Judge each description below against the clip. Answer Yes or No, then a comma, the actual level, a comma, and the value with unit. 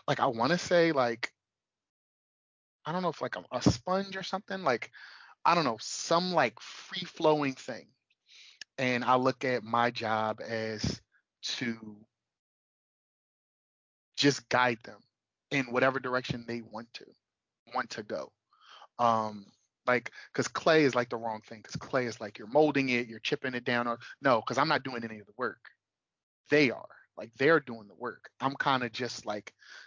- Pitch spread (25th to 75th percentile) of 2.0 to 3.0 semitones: No, average, 4.0 semitones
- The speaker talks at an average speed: Yes, average, 175 wpm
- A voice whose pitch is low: Yes, low, 125 Hz